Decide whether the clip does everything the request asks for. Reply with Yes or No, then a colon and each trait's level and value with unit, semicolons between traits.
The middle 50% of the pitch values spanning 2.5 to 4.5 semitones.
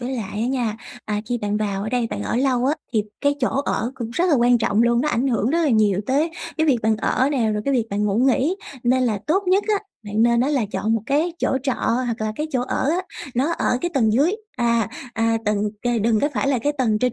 Yes: average, 4.0 semitones